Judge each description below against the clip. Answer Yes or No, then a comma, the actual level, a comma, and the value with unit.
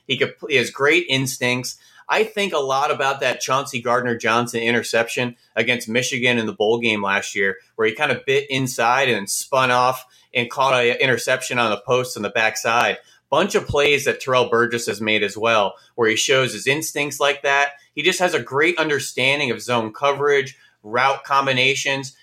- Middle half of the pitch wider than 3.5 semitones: No, narrow, 2.6 semitones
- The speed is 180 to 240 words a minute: Yes, average, 185 wpm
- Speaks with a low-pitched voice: Yes, low, 125 Hz